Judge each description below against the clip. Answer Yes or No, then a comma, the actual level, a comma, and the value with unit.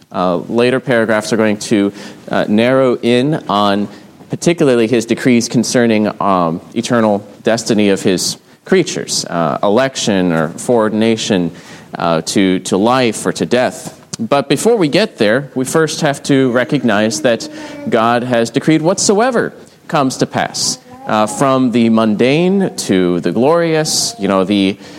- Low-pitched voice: Yes, low, 115 Hz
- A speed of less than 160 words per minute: Yes, average, 140 wpm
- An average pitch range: Yes, average, 4.5 semitones